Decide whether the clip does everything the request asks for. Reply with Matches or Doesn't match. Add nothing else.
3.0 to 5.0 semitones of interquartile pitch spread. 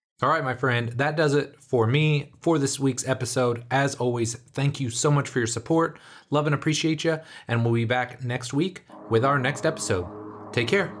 Matches